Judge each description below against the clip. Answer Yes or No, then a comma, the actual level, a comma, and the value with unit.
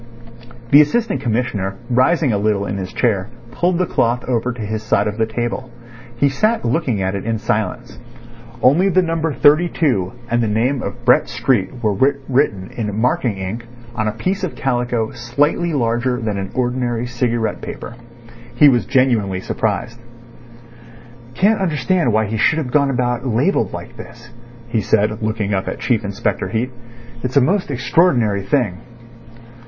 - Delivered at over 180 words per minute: No, average, 165 wpm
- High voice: No, low, 120 Hz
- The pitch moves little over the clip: No, average, 4.0 semitones